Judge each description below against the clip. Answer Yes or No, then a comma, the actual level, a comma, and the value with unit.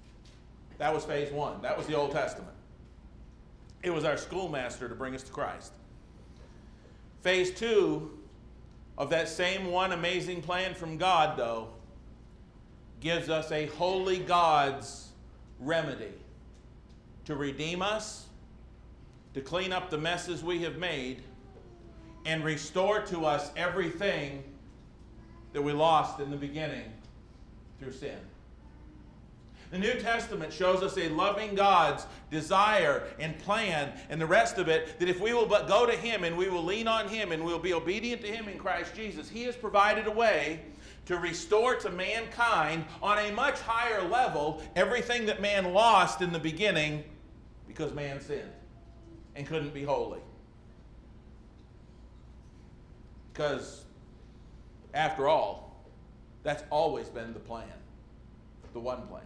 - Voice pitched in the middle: Yes, medium, 165 Hz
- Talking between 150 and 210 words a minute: No, average, 140 wpm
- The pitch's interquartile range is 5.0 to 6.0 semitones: Yes, average, 5.3 semitones